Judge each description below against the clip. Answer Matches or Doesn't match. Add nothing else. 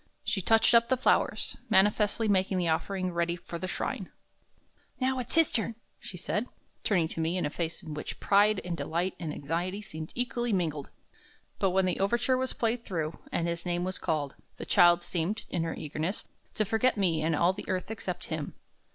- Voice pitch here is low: Doesn't match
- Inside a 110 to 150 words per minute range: Doesn't match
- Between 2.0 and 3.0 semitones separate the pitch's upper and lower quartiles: Doesn't match